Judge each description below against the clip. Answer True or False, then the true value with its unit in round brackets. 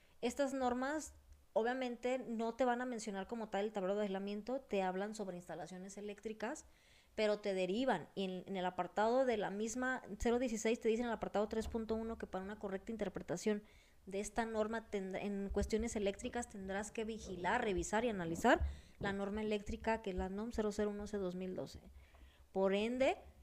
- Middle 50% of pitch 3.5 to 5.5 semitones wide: False (3.0 semitones)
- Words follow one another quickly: False (165 wpm)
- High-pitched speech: True (210 Hz)